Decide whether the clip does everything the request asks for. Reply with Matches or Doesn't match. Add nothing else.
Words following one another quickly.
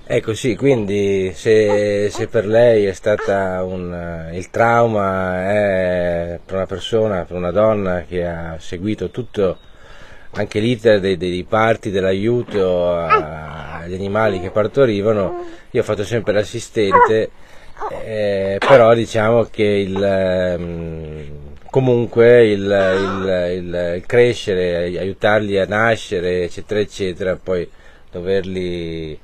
Doesn't match